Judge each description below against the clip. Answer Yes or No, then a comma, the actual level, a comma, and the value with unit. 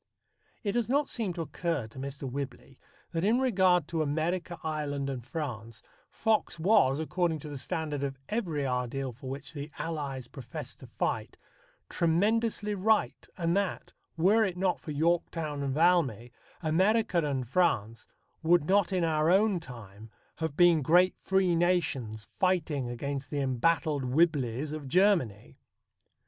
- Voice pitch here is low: No, medium, 160 Hz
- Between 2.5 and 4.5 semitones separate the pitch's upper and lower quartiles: No, average, 4.9 semitones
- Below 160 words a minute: Yes, average, 150 wpm